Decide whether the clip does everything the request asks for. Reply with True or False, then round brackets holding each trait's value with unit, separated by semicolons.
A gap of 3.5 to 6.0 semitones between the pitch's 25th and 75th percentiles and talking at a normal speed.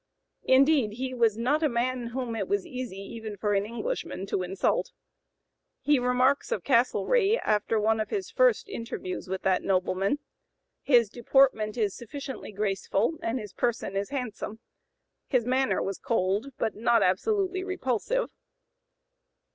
True (4.6 semitones; 145 wpm)